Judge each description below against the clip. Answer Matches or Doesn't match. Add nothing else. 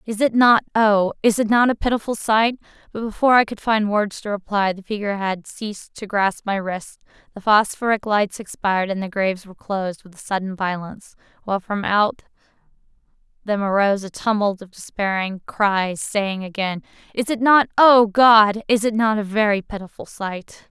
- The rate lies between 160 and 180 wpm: Matches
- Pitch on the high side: Matches